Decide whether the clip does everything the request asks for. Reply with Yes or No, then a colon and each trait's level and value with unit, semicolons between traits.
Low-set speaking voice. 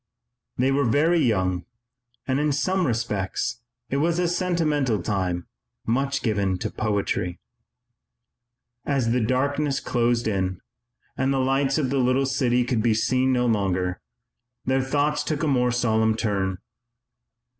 Yes: low, 125 Hz